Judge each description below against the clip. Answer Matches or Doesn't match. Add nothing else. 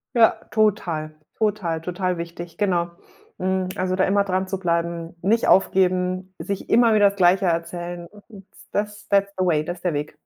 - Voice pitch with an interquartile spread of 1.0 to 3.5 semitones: Matches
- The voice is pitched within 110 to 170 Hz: Doesn't match